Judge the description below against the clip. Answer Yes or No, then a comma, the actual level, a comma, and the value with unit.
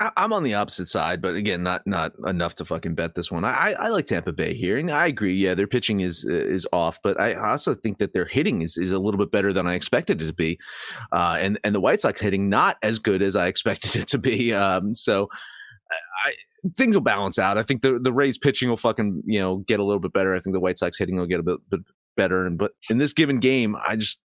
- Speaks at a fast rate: Yes, fast, 265 wpm